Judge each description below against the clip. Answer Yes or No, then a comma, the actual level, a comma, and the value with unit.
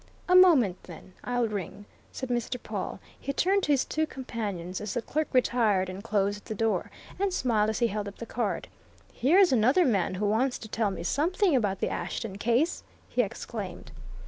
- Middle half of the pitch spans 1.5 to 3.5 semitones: No, average, 5.2 semitones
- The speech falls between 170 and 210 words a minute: Yes, average, 190 wpm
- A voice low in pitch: No, high, 230 Hz